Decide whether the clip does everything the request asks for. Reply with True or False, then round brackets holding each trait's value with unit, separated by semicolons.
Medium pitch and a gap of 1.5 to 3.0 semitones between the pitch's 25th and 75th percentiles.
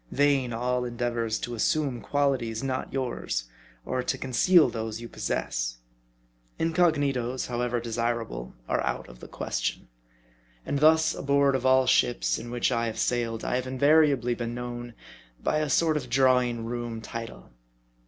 False (125 Hz; 2.7 semitones)